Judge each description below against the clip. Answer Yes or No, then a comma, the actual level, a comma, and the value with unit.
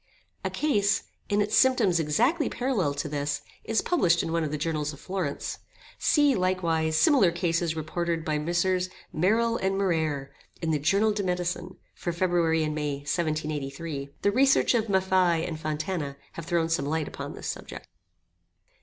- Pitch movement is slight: No, average, 3.9 semitones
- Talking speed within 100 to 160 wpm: No, average, 170 wpm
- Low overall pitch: No, medium, 170 Hz